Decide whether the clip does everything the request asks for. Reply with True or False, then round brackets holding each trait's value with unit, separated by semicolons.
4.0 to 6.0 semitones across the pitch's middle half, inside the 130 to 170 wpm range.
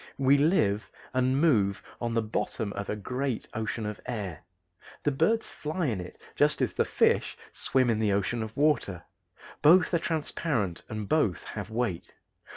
True (5.5 semitones; 165 wpm)